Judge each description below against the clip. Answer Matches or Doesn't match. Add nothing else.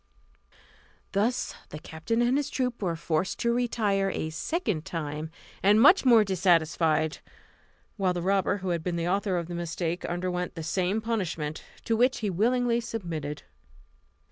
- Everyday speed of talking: Matches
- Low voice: Doesn't match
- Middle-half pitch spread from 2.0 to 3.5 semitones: Doesn't match